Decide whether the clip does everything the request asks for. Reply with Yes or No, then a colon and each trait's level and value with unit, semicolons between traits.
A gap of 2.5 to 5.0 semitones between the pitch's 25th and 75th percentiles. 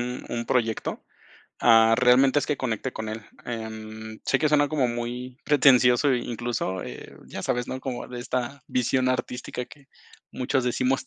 No: narrow, 1.9 semitones